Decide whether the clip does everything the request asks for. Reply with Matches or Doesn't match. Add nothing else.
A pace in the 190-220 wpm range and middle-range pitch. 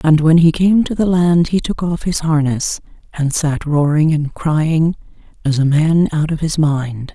Matches